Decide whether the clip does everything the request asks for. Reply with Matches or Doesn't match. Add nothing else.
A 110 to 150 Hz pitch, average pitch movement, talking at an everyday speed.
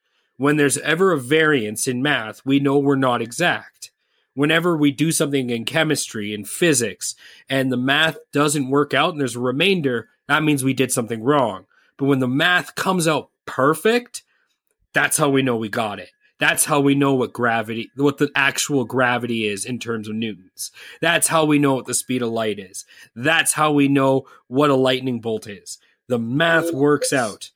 Matches